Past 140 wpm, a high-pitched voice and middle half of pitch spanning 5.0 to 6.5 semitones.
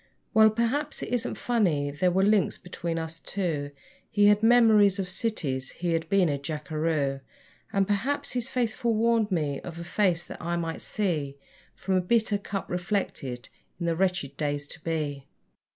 No: average, 170 wpm; medium, 180 Hz; wide, 5.4 semitones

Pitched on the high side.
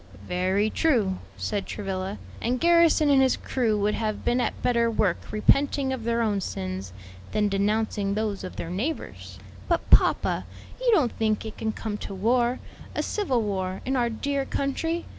Yes: high, 220 Hz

